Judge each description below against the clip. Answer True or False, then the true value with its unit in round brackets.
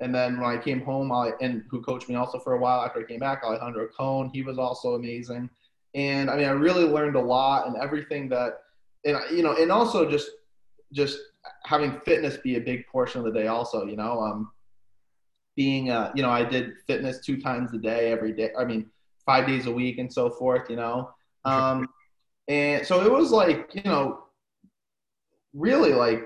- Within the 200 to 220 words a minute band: True (205 wpm)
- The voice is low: True (125 Hz)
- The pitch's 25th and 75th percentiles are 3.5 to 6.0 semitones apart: False (2.4 semitones)